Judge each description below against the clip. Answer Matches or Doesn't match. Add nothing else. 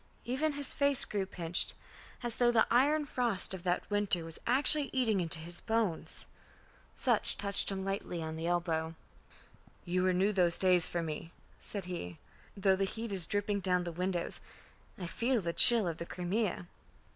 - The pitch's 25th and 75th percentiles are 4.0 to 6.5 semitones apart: Matches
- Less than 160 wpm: Doesn't match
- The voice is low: Doesn't match